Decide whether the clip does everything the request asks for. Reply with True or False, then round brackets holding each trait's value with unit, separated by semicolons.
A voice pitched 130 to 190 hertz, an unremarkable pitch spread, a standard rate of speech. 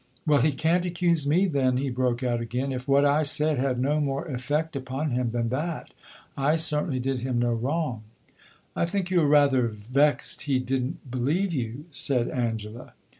True (135 Hz; 3.3 semitones; 185 wpm)